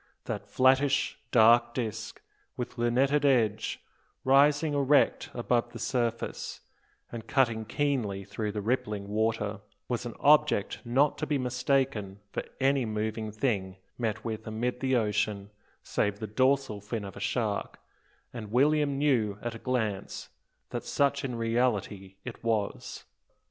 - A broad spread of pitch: No, average, 3.9 semitones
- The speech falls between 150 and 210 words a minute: No, average, 140 wpm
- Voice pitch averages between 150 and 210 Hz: No, low, 115 Hz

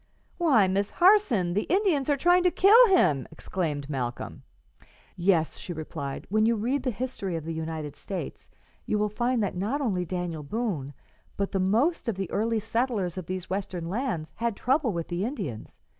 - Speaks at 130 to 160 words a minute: No, average, 180 wpm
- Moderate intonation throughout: No, wide, 6.7 semitones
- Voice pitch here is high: Yes, high, 200 Hz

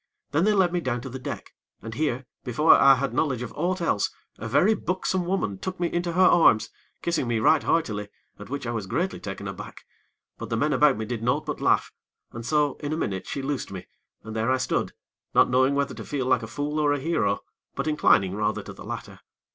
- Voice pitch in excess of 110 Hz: Yes, low, 135 Hz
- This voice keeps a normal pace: No, fast, 230 wpm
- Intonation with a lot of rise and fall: Yes, wide, 6.1 semitones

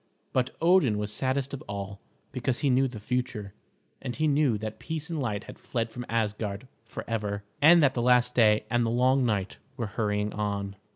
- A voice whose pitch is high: No, low, 120 Hz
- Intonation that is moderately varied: Yes, average, 3.8 semitones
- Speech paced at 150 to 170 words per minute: No, average, 190 wpm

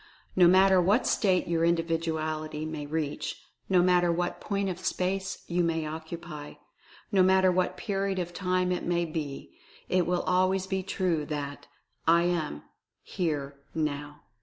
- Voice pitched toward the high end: No, medium, 175 Hz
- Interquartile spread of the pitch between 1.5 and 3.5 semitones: Yes, average, 2.9 semitones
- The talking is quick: No, average, 155 wpm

